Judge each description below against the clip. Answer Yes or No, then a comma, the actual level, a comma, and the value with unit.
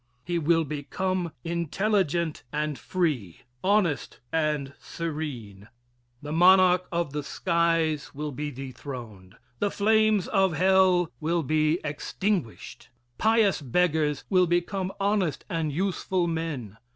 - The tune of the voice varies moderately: Yes, average, 3.9 semitones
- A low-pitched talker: No, medium, 165 Hz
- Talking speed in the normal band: No, slow, 115 wpm